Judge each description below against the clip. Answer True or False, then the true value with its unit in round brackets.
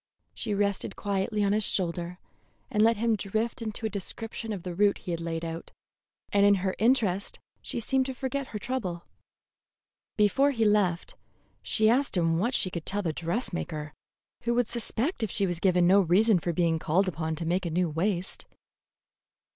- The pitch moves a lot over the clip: False (4.3 semitones)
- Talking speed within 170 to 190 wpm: True (185 wpm)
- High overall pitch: True (200 Hz)